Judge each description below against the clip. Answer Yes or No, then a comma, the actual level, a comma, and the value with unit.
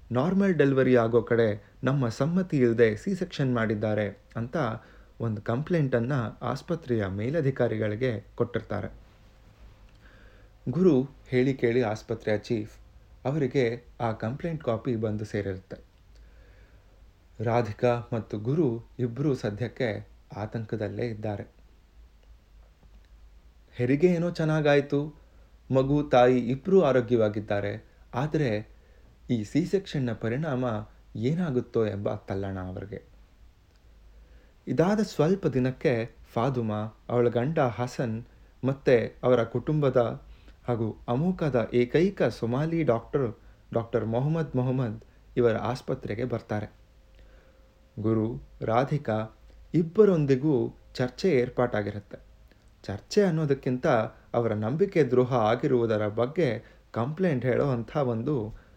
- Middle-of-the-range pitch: No, low, 120 Hz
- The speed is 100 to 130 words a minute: No, average, 90 wpm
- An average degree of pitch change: Yes, average, 4.0 semitones